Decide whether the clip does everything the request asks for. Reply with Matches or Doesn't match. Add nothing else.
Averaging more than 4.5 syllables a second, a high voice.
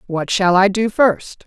Doesn't match